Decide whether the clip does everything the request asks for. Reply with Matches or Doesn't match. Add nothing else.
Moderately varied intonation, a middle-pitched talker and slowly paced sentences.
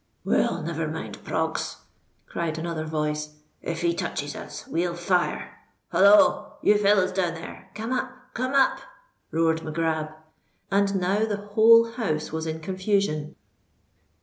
Matches